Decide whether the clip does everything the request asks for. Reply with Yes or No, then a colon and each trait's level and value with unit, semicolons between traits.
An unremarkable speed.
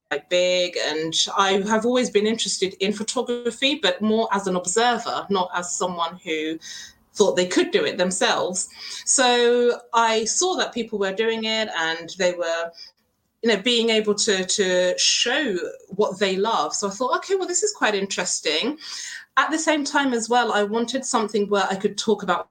Yes: average, 185 wpm